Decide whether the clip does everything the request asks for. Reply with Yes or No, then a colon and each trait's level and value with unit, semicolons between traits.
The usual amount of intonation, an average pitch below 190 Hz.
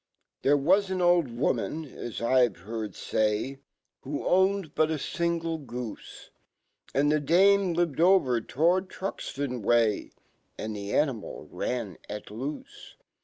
No: wide, 6.5 semitones; medium, 140 Hz